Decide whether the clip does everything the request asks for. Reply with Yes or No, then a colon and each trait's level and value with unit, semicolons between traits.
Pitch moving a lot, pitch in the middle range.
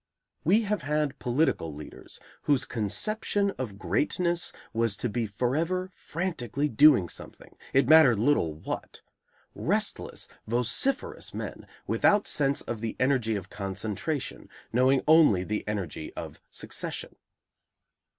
No: wide, 6.9 semitones; low, 130 Hz